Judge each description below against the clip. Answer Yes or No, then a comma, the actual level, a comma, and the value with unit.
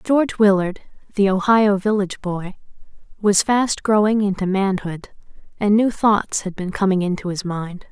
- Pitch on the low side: No, high, 200 Hz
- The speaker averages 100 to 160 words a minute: Yes, average, 150 wpm